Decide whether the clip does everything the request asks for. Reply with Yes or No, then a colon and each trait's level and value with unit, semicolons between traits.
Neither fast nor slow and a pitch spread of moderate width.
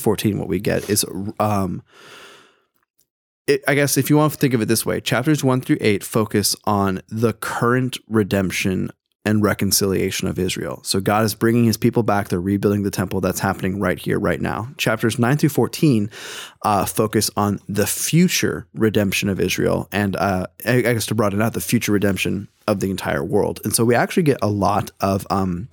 Yes: average, 195 wpm; average, 3.7 semitones